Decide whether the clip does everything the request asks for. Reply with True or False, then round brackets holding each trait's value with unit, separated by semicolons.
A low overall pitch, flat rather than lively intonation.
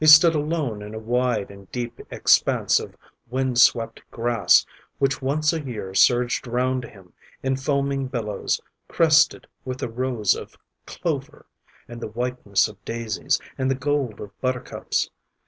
False (125 Hz; 3.2 semitones)